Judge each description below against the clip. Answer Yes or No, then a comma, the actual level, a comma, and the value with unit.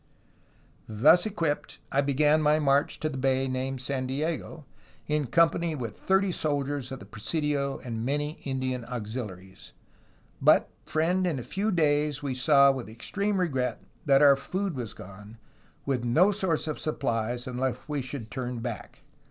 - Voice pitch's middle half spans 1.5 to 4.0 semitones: Yes, average, 3.6 semitones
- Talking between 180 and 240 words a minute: No, average, 155 wpm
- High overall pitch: No, medium, 140 Hz